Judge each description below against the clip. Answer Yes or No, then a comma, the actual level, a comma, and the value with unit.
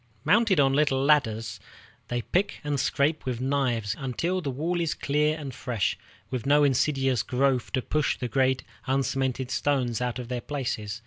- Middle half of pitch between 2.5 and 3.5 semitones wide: Yes, average, 2.9 semitones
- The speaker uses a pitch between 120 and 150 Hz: Yes, low, 135 Hz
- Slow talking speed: No, average, 170 wpm